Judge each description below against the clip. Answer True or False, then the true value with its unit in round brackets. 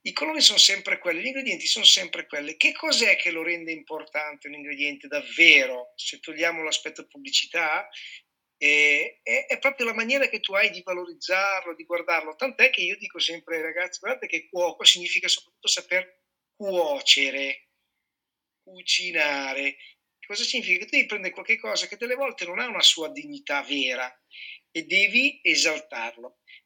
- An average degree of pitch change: False (5.9 semitones)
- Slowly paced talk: False (160 wpm)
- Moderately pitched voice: True (175 Hz)